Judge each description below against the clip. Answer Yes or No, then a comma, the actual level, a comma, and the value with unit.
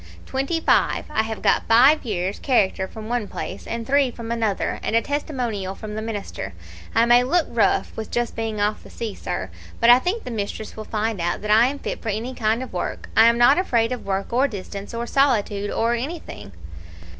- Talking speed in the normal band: No, fast, 215 wpm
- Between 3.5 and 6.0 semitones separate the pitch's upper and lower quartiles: No, average, 3.1 semitones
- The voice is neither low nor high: No, high, 230 Hz